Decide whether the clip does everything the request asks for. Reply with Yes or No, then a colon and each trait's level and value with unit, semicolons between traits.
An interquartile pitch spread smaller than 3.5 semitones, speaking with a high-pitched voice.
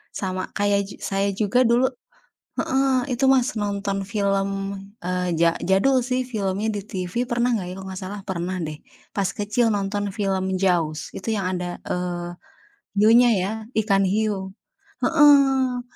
No: average, 4.0 semitones; high, 200 Hz